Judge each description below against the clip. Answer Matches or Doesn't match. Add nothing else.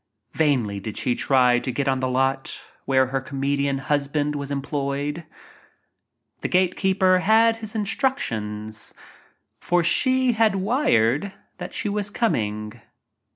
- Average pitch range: Doesn't match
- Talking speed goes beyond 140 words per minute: Doesn't match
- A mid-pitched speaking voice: Matches